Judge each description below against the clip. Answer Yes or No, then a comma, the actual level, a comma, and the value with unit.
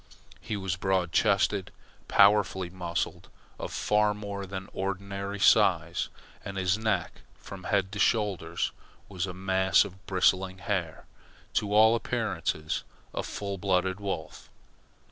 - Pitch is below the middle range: Yes, very low, 95 Hz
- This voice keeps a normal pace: No, slow, 125 wpm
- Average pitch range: No, narrow, 1.6 semitones